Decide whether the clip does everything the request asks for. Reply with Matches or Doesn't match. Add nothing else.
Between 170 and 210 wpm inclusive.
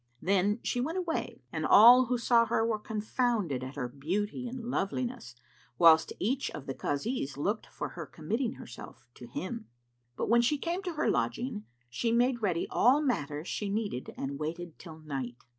Matches